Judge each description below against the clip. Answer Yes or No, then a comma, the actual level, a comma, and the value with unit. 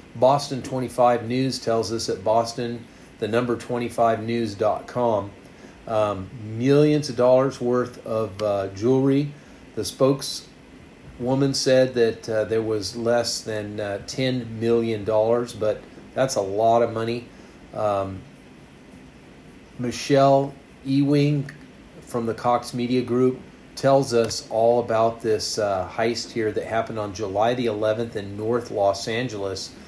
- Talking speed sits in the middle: No, slow, 125 wpm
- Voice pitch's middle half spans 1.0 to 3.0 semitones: Yes, narrow, 2.5 semitones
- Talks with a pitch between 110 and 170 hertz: Yes, low, 115 Hz